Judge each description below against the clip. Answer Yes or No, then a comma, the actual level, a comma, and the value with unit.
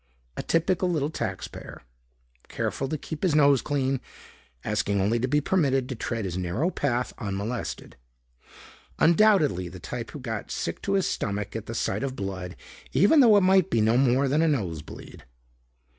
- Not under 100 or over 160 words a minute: No, average, 175 wpm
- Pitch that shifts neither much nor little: No, wide, 6.9 semitones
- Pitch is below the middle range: Yes, low, 130 Hz